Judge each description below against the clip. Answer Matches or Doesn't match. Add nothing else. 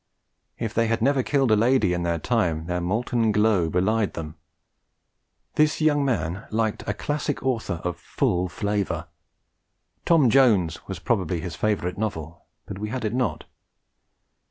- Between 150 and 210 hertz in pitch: Doesn't match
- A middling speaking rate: Matches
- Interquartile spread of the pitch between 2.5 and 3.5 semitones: Doesn't match